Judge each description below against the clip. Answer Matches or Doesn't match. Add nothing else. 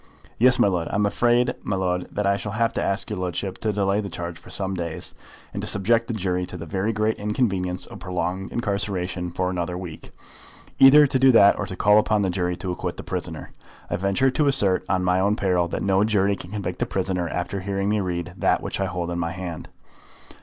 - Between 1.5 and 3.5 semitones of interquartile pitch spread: Matches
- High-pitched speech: Doesn't match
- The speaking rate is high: Matches